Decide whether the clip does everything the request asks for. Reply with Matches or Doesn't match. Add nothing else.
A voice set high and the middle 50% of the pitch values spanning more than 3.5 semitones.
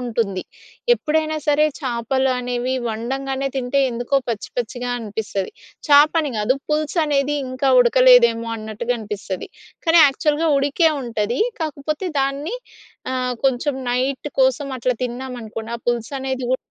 Doesn't match